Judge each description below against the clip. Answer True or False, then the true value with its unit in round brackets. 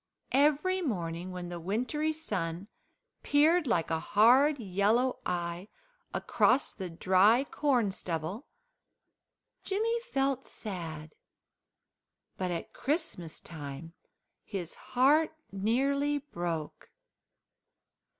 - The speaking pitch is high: True (210 Hz)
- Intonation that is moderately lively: False (8.5 semitones)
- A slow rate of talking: True (90 wpm)